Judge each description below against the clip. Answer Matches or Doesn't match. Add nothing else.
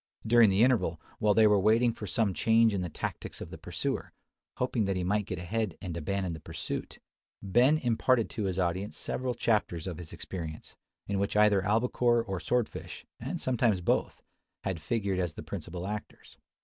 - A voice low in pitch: Matches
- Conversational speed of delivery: Matches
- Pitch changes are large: Doesn't match